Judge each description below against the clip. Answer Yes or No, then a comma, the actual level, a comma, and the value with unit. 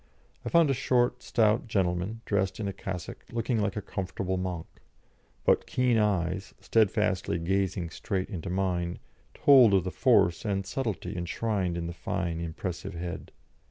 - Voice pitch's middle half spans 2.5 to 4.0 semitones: Yes, average, 3.7 semitones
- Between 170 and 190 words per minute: No, average, 155 wpm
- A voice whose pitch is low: Yes, very low, 95 Hz